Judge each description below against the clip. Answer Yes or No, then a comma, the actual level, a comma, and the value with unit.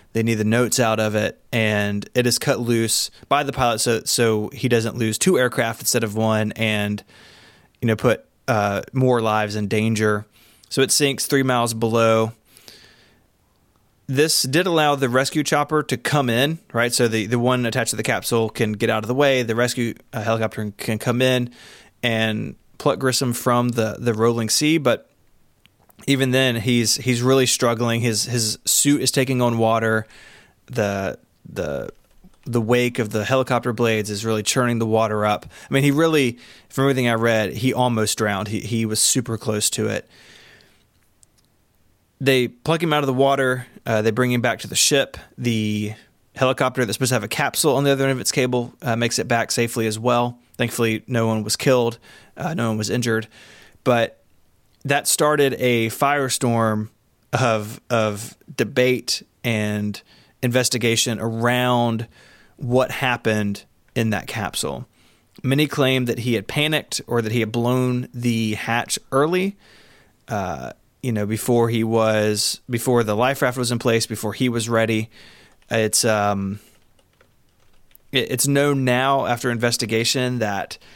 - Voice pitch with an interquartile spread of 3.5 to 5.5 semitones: No, average, 2.7 semitones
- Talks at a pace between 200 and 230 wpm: No, average, 170 wpm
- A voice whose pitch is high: No, low, 120 Hz